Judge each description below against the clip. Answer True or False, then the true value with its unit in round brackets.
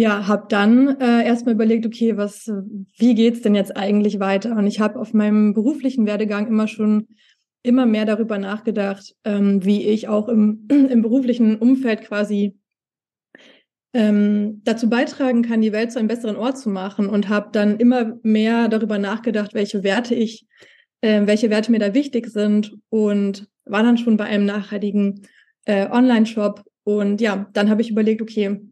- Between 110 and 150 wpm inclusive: False (175 wpm)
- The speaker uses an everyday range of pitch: False (2.0 semitones)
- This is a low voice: False (215 Hz)